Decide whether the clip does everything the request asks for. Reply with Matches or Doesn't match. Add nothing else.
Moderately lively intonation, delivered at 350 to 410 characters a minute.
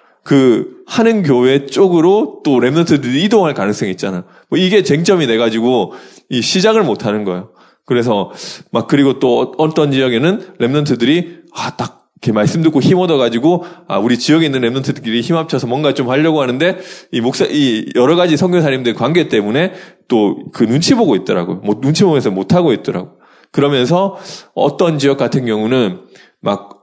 Doesn't match